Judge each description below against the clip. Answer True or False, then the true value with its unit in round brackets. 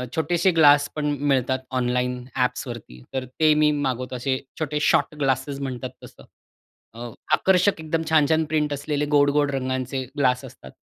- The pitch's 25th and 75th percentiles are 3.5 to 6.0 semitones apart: False (2.8 semitones)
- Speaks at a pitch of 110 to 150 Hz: True (140 Hz)